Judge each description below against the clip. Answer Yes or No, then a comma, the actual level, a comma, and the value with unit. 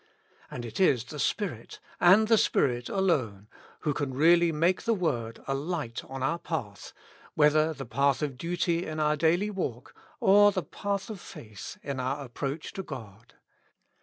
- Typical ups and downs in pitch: No, wide, 5.8 semitones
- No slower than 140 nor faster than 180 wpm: Yes, average, 165 wpm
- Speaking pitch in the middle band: Yes, medium, 150 Hz